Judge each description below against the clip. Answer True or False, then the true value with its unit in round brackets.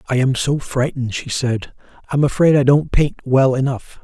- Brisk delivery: False (180 wpm)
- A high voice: False (135 Hz)